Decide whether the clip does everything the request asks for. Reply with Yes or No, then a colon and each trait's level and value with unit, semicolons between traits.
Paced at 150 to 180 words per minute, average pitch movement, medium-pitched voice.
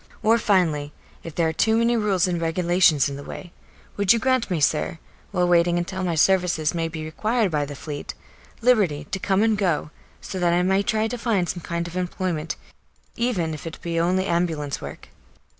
No: average, 200 wpm; average, 3.6 semitones; medium, 175 Hz